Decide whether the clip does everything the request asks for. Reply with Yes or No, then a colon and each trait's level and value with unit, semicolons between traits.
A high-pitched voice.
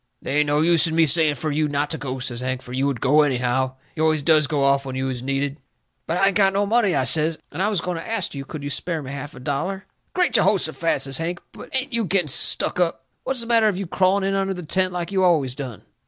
No: medium, 155 Hz